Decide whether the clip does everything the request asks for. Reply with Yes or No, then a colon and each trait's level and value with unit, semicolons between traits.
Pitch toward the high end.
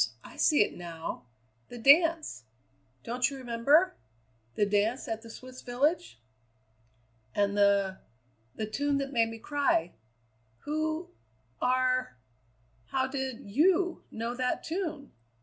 Yes: very high, 255 Hz